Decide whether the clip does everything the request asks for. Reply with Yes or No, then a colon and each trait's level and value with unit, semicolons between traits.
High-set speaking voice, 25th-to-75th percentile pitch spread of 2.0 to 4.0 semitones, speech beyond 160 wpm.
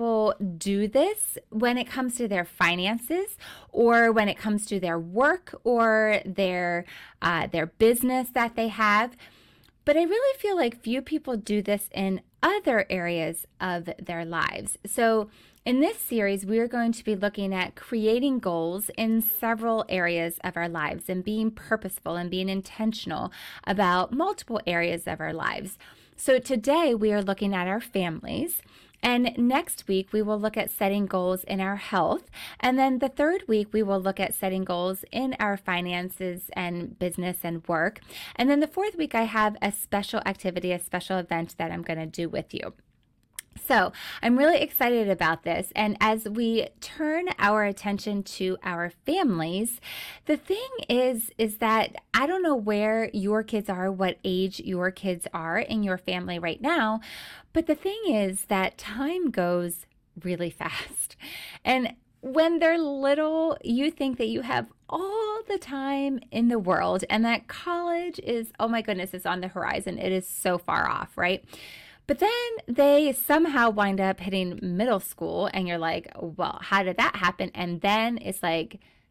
No: high, 215 Hz; wide, 5.4 semitones; average, 170 wpm